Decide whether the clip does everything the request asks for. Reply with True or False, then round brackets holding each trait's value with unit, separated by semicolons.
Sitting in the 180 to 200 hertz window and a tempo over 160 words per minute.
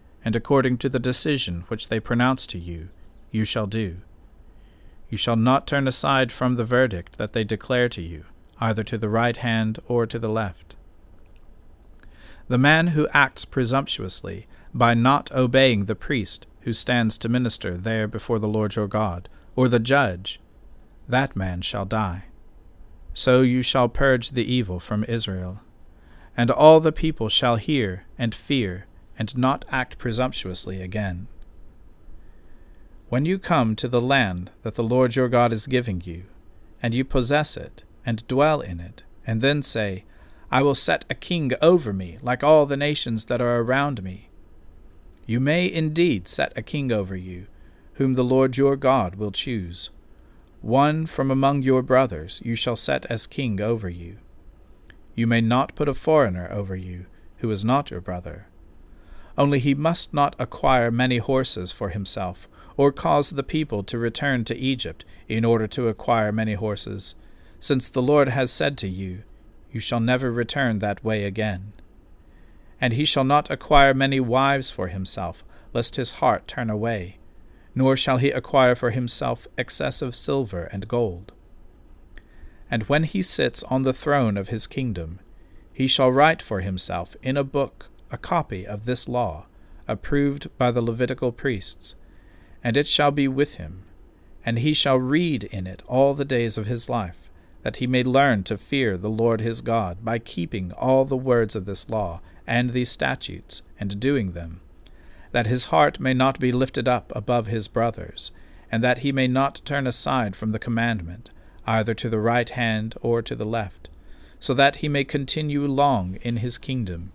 False (115 Hz; 170 wpm)